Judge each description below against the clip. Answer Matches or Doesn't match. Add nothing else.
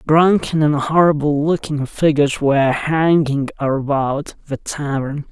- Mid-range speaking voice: Matches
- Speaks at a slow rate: Matches